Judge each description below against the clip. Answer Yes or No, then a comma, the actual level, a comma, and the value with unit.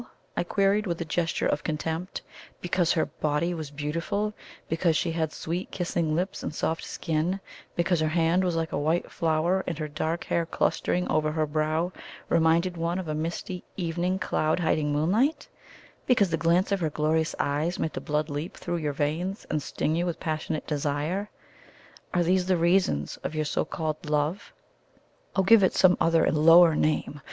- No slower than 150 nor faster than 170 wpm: No, average, 185 wpm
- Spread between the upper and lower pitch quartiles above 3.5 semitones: No, narrow, 2.5 semitones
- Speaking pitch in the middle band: Yes, medium, 165 Hz